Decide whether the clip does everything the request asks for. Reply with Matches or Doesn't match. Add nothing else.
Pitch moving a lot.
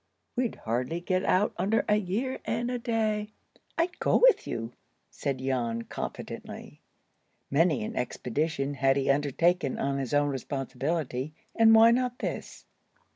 Matches